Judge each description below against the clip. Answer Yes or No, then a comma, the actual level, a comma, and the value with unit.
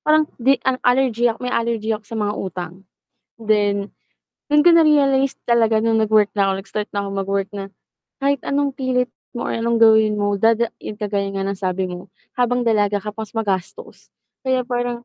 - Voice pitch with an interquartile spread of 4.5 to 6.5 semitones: No, average, 3.5 semitones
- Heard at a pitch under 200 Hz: No, high, 225 Hz